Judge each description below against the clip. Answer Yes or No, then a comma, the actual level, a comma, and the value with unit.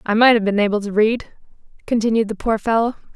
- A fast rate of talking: Yes, fast, 210 wpm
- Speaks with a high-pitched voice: Yes, high, 220 Hz